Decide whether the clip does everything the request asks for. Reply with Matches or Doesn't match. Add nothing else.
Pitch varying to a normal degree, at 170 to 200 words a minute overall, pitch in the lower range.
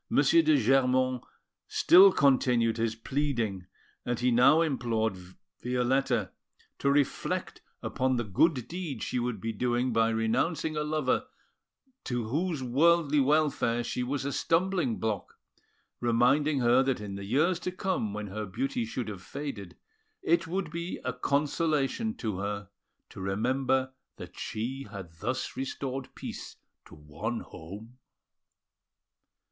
Doesn't match